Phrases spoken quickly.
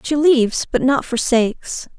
No: average, 150 wpm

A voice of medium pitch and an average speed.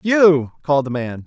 Yes: medium, 150 Hz; average, 190 wpm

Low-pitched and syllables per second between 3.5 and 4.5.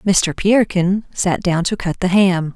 No: medium, 185 Hz; 4.1 syllables/s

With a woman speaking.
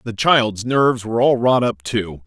No: male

